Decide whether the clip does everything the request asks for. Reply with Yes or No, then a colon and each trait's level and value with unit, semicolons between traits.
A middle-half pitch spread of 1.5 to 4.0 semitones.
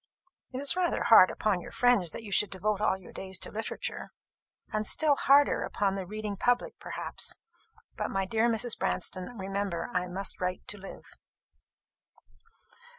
Yes: average, 3.7 semitones